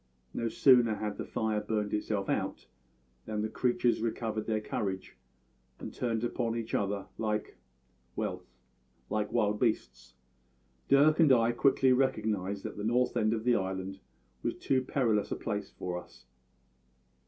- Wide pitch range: No, average, 2.7 semitones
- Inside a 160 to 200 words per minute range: No, average, 150 wpm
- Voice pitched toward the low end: Yes, low, 110 Hz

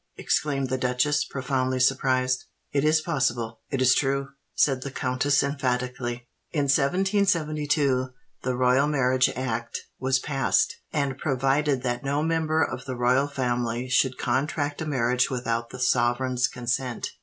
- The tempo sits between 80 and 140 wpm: Yes, slow, 135 wpm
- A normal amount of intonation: No, narrow, 2.2 semitones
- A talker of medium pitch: No, low, 130 Hz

